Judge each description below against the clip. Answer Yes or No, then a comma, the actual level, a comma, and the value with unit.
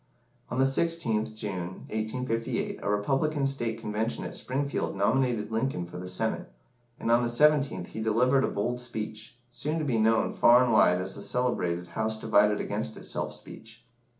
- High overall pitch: No, low, 115 Hz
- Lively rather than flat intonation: No, average, 3.2 semitones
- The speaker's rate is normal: Yes, average, 170 wpm